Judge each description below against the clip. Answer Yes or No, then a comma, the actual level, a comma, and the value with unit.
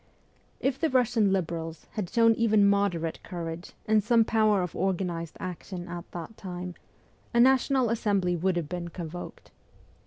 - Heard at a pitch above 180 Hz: Yes, high, 190 Hz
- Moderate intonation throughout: Yes, average, 4.2 semitones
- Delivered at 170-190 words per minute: No, average, 155 wpm